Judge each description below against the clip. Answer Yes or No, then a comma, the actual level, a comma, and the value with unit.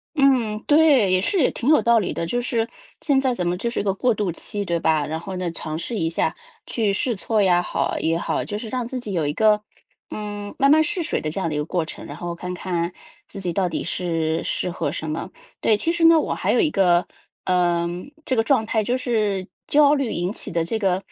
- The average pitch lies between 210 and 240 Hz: No, high, 200 Hz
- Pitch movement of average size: No, wide, 5.8 semitones